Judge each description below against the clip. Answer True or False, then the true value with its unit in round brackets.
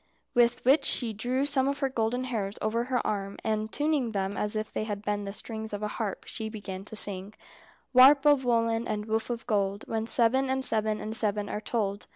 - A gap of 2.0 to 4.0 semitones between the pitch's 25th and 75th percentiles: True (2.9 semitones)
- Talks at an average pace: False (215 wpm)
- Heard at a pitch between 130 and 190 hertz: False (220 Hz)